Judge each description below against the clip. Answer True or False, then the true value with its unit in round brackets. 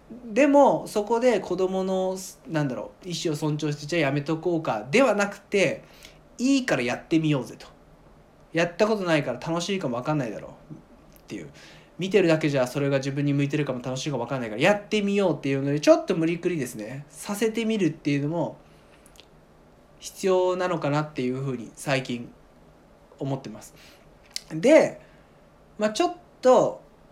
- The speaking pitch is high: False (165 Hz)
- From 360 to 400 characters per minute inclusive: True (365 characters per minute)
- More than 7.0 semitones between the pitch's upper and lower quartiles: False (6.1 semitones)